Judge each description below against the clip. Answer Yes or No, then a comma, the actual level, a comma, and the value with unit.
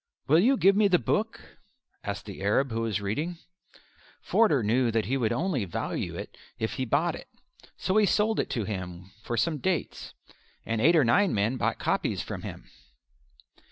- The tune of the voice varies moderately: No, wide, 8.0 semitones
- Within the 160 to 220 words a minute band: Yes, average, 185 wpm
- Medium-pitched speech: No, low, 130 Hz